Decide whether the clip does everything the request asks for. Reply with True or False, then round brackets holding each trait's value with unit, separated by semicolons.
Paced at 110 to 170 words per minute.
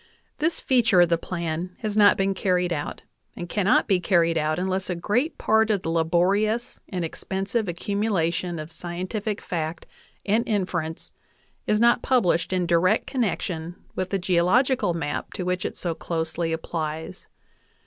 True (160 wpm)